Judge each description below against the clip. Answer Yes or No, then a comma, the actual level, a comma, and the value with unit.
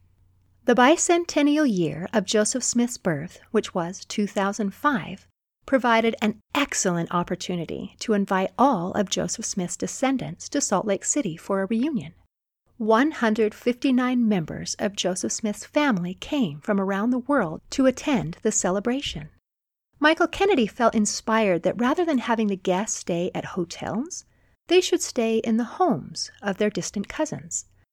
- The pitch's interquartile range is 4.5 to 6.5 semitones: Yes, wide, 5.4 semitones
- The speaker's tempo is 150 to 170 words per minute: No, average, 140 wpm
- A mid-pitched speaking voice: No, high, 220 Hz